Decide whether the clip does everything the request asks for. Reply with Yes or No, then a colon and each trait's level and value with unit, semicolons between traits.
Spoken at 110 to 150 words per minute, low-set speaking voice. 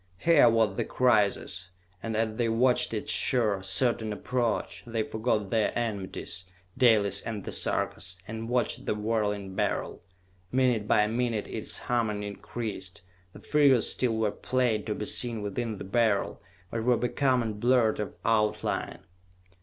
Yes: average, 145 wpm; low, 110 Hz